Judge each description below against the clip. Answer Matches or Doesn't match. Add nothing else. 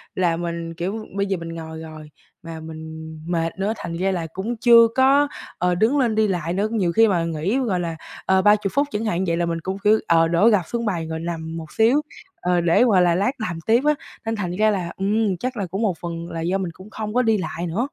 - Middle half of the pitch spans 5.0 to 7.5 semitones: Doesn't match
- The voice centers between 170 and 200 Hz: Matches